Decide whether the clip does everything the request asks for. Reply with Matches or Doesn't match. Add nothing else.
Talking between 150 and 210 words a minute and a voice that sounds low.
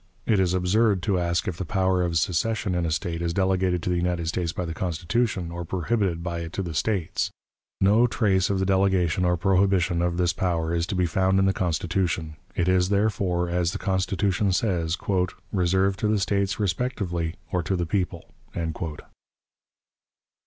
Matches